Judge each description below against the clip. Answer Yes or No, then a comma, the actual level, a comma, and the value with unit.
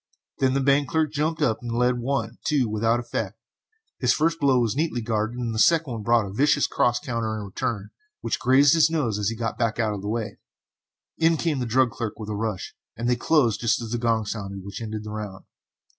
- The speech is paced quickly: Yes, fast, 230 wpm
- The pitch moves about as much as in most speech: Yes, average, 3.9 semitones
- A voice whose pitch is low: Yes, low, 120 Hz